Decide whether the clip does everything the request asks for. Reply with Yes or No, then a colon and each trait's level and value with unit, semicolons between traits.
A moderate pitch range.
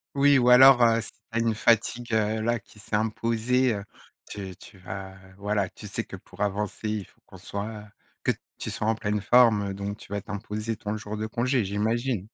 No: narrow, 2.2 semitones